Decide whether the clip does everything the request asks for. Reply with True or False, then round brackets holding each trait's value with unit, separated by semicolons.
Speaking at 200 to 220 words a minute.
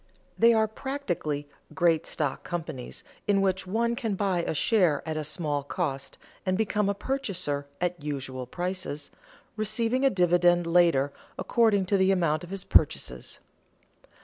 False (150 wpm)